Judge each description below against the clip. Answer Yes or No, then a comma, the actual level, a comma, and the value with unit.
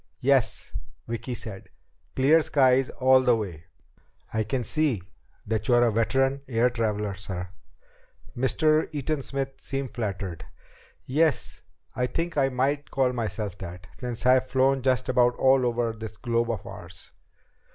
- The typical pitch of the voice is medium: No, low, 125 Hz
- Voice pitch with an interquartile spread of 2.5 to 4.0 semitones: Yes, average, 3.3 semitones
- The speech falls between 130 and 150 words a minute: Yes, average, 140 wpm